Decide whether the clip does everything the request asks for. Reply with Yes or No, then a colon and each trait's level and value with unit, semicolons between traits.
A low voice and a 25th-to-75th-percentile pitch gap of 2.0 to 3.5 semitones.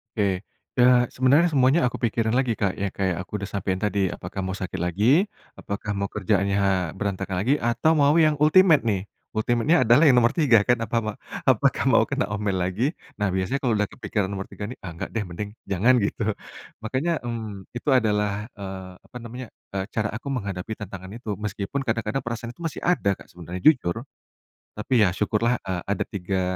No: low, 105 Hz; average, 4.0 semitones